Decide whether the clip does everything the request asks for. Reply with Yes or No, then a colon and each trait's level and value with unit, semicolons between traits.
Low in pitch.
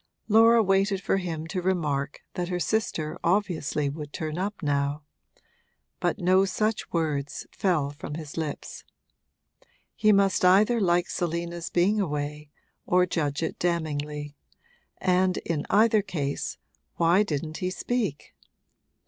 No: medium, 175 Hz